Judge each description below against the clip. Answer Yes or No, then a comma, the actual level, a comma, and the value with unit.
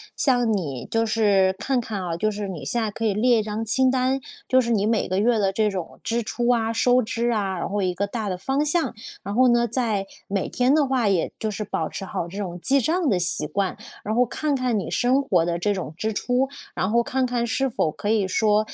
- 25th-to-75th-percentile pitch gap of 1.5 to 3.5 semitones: No, average, 4.1 semitones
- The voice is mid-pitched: No, high, 220 Hz